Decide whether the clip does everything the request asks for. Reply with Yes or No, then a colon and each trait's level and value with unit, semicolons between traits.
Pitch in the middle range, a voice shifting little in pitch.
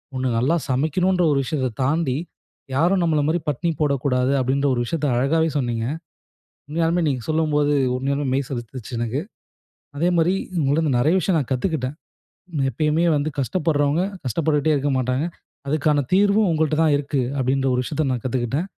No: medium, 145 Hz; average, 3.6 semitones